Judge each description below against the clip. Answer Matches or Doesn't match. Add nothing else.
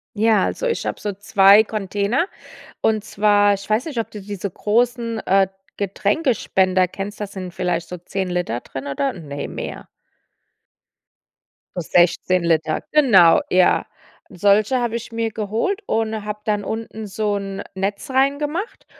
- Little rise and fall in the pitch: Doesn't match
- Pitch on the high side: Matches